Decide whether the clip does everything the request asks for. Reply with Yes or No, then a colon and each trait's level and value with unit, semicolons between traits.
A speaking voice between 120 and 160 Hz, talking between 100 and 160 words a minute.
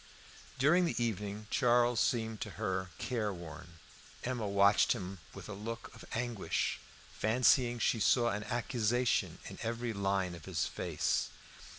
No: low, 110 Hz; slow, 135 wpm